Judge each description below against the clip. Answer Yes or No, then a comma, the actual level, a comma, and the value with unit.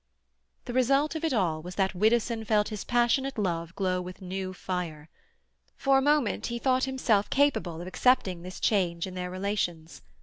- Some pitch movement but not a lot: No, wide, 5.7 semitones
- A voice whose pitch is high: Yes, high, 200 Hz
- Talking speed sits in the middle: Yes, average, 175 wpm